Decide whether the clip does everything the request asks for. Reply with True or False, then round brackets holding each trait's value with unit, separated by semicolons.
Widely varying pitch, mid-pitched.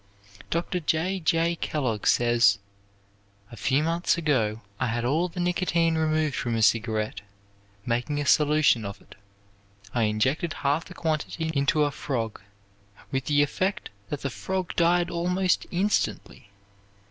True (6.0 semitones; 150 Hz)